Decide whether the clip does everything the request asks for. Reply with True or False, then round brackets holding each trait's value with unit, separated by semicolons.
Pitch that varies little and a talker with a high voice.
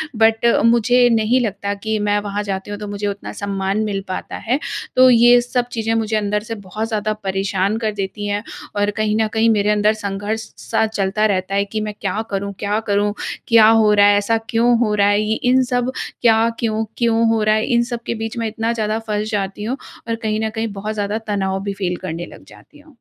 True (1.8 semitones; 215 Hz)